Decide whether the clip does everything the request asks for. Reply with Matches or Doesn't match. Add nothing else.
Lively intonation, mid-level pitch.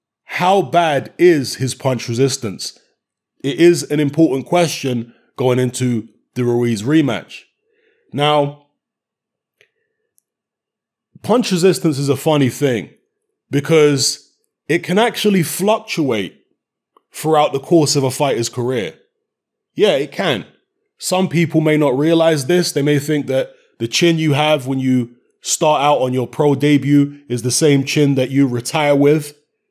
Doesn't match